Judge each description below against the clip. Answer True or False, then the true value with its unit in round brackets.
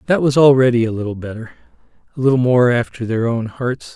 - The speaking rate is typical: True (195 wpm)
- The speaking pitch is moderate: False (120 Hz)